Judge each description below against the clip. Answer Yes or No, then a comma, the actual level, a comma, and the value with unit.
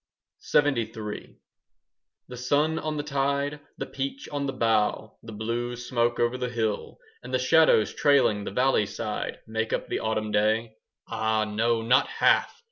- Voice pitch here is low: Yes, low, 120 Hz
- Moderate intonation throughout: Yes, average, 3.7 semitones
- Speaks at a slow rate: No, average, 155 wpm